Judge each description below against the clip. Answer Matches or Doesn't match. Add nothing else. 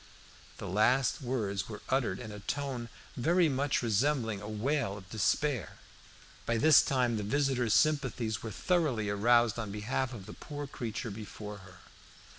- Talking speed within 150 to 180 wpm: Matches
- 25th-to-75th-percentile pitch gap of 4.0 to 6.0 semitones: Matches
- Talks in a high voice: Doesn't match